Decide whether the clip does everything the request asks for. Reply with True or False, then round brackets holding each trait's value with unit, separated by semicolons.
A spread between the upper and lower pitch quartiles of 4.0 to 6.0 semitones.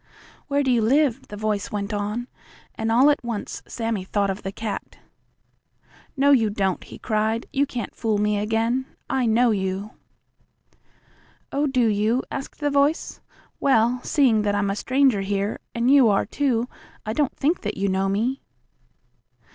True (4.3 semitones)